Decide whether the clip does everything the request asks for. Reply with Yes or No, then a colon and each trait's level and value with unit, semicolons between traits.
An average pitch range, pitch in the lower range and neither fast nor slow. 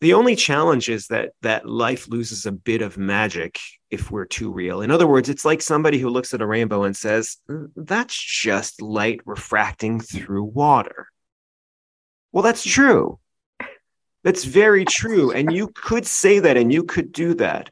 No: wide, 7.6 semitones; low, 125 Hz; average, 175 wpm